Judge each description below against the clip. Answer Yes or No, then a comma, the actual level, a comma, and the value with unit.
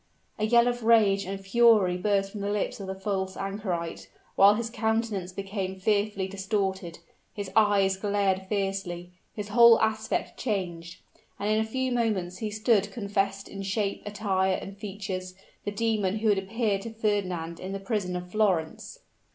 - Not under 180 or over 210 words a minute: No, average, 165 wpm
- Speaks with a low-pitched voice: No, high, 200 Hz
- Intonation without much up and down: Yes, narrow, 2.1 semitones